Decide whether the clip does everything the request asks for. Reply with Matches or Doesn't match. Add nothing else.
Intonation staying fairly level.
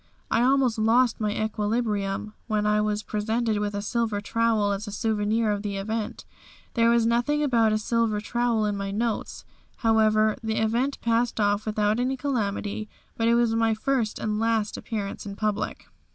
Matches